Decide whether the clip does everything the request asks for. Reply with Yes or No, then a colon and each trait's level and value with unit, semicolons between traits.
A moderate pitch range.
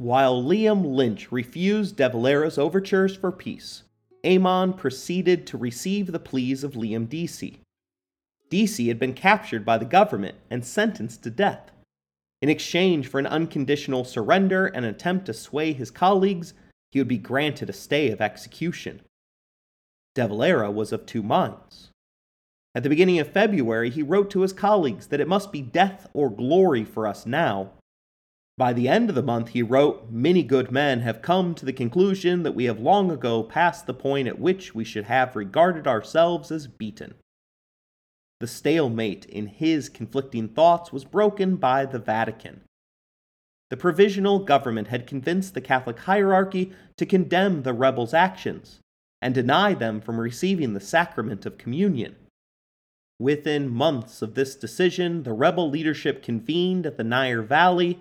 No: wide, 7.1 semitones